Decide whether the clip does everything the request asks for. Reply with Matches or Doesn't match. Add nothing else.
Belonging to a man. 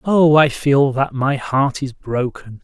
Matches